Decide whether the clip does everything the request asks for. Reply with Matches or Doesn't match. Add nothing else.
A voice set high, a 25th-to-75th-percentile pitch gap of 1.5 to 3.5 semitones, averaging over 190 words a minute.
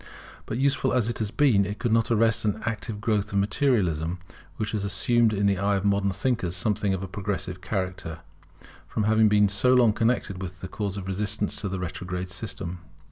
Doesn't match